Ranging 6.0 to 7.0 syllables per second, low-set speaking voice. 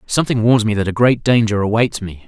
Yes: 6.1 syllables/s; low, 110 Hz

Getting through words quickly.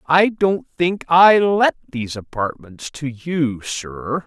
No: average, 140 wpm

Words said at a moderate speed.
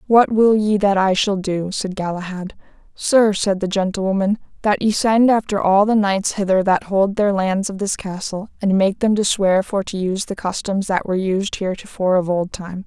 No: fast, 210 wpm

